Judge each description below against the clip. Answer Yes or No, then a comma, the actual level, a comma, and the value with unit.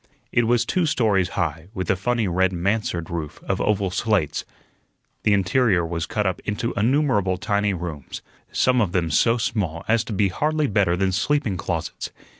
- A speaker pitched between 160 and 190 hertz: No, low, 100 Hz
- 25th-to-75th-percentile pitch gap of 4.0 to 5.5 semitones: Yes, average, 4.4 semitones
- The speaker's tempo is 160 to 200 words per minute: Yes, average, 175 wpm